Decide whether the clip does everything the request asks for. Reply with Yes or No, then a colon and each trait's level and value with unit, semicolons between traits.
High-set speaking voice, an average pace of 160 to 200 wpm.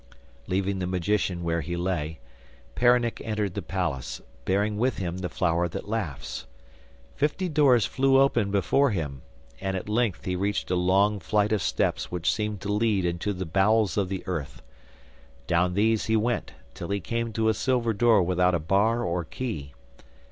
No: low, 100 Hz; average, 175 wpm